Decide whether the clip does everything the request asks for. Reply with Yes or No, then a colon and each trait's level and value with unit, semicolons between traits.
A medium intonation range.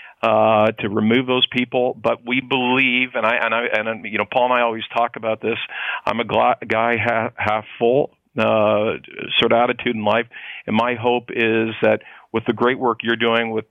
No: narrow, 1.8 semitones